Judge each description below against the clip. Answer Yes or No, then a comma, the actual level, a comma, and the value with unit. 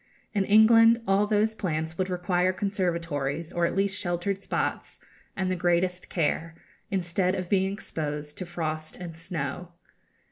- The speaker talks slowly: No, average, 145 wpm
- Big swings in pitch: No, average, 2.8 semitones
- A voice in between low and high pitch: Yes, medium, 180 Hz